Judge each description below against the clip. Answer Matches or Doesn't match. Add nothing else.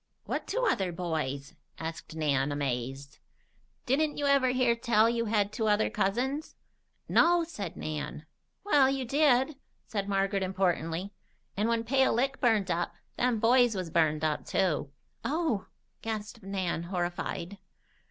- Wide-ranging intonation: Matches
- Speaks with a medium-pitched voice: Doesn't match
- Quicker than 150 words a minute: Doesn't match